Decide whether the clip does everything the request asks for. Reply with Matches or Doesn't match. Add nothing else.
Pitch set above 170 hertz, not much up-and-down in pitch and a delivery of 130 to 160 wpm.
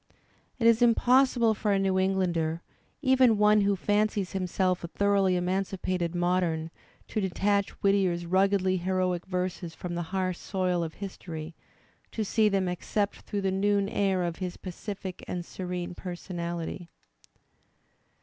Matches